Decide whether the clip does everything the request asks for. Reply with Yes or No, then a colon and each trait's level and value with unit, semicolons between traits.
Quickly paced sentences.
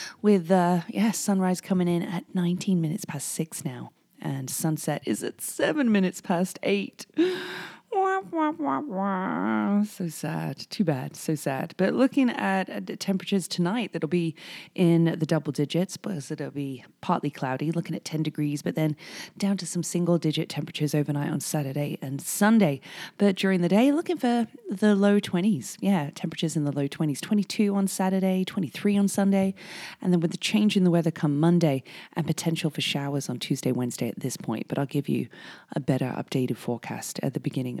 No: average, 180 wpm